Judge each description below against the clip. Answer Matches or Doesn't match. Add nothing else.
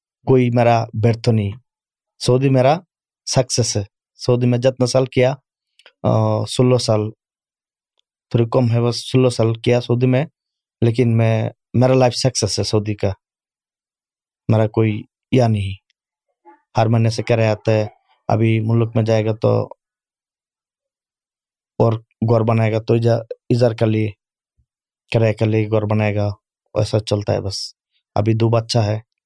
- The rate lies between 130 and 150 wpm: Matches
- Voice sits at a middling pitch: Doesn't match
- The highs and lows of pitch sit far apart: Doesn't match